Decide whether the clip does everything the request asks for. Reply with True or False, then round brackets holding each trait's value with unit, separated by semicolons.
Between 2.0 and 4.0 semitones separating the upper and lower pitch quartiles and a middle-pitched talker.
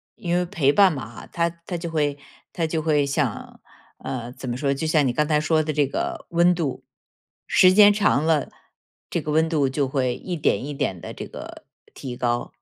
True (3.6 semitones; 150 Hz)